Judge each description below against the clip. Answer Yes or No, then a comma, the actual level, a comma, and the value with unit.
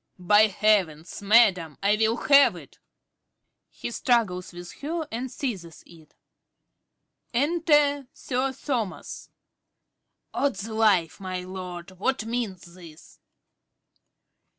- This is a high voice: Yes, high, 210 Hz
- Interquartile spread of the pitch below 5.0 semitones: No, wide, 5.6 semitones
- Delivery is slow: Yes, slow, 110 wpm